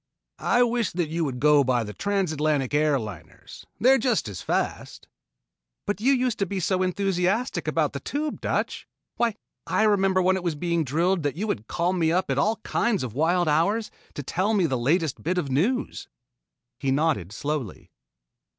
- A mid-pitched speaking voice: Yes, medium, 170 Hz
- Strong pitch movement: Yes, wide, 5.7 semitones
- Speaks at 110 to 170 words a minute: No, average, 190 wpm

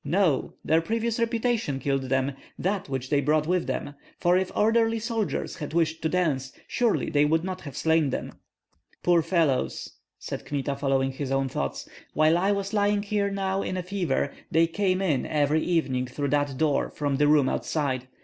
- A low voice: No, medium, 160 Hz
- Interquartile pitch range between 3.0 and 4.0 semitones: No, wide, 5.5 semitones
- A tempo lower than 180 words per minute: No, average, 185 wpm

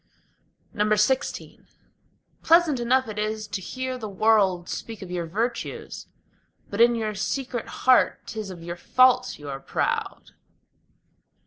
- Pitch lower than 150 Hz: No, high, 215 Hz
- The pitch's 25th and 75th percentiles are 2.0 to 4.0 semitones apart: No, average, 4.6 semitones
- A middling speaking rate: No, slow, 130 wpm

